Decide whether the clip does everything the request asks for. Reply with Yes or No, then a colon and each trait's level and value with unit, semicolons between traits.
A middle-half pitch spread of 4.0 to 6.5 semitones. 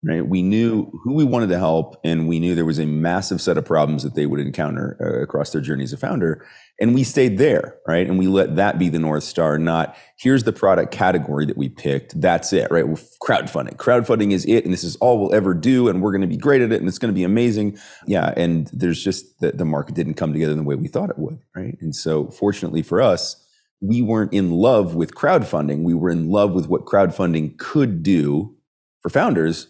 Yes: average, 4.4 semitones